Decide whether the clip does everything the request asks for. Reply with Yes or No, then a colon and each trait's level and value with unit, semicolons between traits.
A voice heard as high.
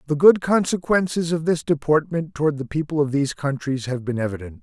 No: medium, 150 Hz